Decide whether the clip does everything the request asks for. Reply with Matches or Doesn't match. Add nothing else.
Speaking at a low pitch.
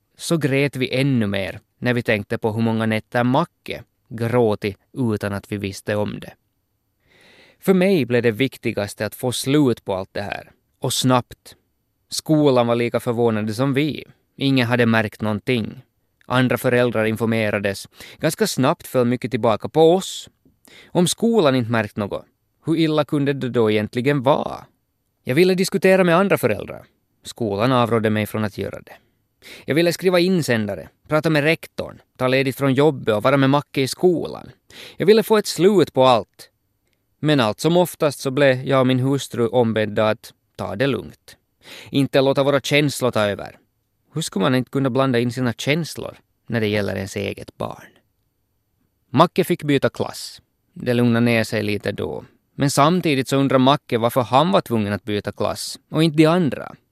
Matches